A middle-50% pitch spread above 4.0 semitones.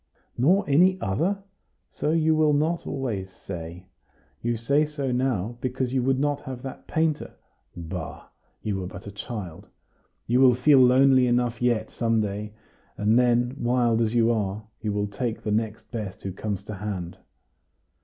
Yes: average, 4.4 semitones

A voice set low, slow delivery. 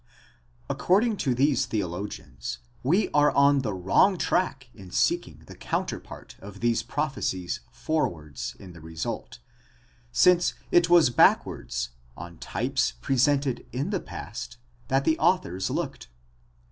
Yes: low, 125 Hz; slow, 130 wpm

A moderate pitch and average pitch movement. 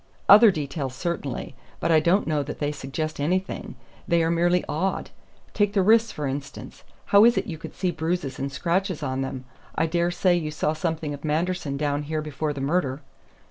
Yes: medium, 160 Hz; average, 3.7 semitones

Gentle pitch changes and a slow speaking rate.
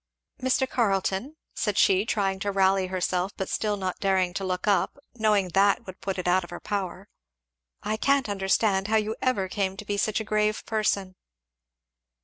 No: narrow, 2.2 semitones; average, 180 wpm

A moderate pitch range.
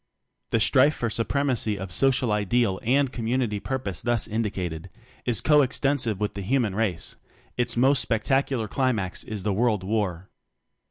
Yes: average, 4.1 semitones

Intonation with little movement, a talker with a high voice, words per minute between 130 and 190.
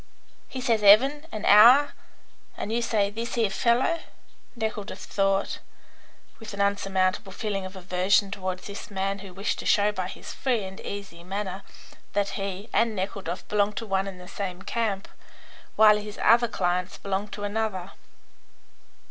Yes: narrow, 2.2 semitones; high, 200 Hz; average, 155 wpm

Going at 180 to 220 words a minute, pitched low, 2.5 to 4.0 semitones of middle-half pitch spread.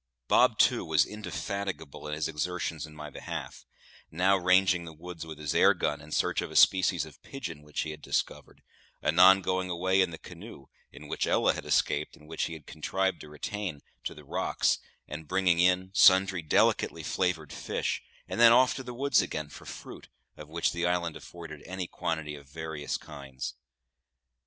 Yes: average, 185 wpm; very low, 85 Hz; average, 3.6 semitones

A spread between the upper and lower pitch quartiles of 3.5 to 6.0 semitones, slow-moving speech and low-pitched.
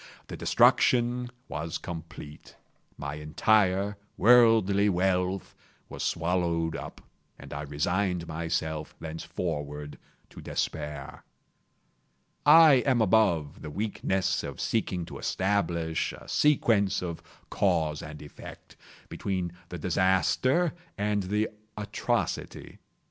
Yes: average, 4.5 semitones; slow, 100 wpm; very low, 90 Hz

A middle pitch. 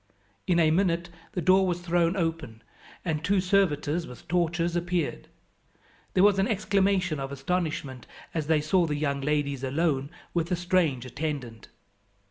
Yes: medium, 165 Hz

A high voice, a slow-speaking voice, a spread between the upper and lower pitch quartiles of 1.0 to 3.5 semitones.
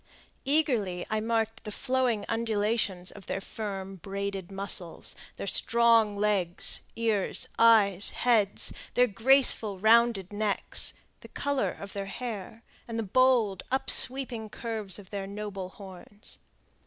Yes: high, 210 Hz; slow, 125 wpm; average, 2.9 semitones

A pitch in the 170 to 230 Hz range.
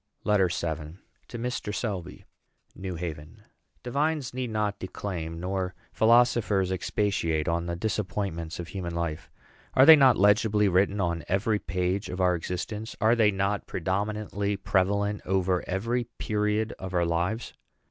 No: very low, 95 Hz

